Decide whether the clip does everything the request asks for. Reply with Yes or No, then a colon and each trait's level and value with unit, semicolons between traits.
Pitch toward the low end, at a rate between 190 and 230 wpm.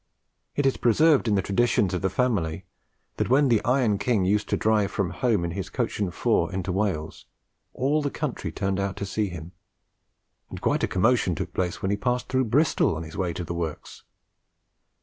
Yes: low, 100 Hz; fast, 205 wpm